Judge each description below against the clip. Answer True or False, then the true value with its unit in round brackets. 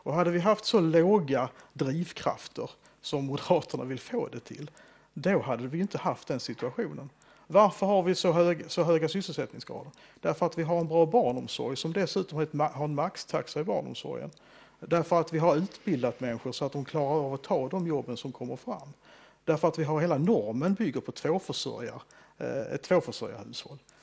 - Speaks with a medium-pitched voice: True (165 Hz)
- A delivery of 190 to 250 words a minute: False (180 wpm)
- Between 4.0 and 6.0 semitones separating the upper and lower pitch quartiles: False (3.6 semitones)